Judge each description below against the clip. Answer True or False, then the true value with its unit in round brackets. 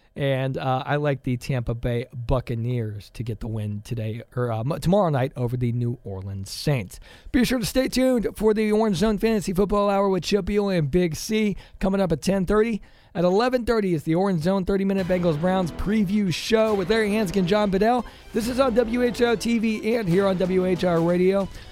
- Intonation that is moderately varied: False (8.5 semitones)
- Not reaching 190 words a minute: False (195 wpm)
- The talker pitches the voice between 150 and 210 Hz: True (190 Hz)